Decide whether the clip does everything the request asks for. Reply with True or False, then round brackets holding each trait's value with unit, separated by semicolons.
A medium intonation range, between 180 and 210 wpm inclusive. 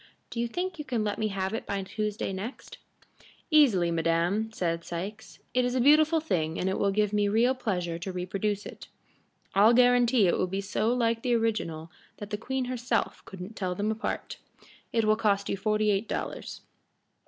True (3.9 semitones; 190 wpm)